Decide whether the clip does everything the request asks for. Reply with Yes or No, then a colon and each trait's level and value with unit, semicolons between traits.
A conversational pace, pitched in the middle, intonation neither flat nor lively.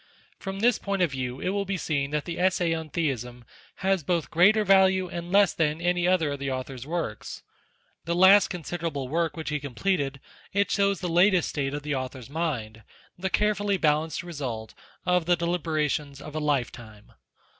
Yes: average, 185 wpm; medium, 165 Hz; average, 4.7 semitones